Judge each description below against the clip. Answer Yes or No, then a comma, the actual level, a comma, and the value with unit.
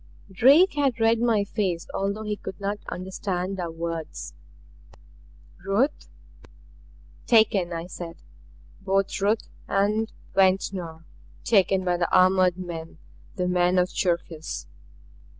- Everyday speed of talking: No, slow, 115 wpm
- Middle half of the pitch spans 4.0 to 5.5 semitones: No, average, 2.8 semitones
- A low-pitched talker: No, high, 190 Hz